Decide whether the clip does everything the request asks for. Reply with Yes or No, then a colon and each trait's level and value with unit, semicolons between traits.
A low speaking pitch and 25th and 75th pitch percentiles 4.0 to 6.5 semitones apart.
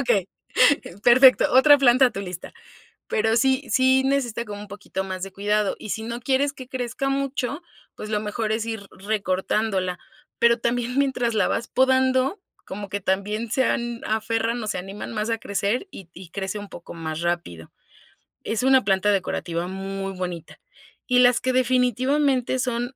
No: high, 225 Hz; average, 4.5 semitones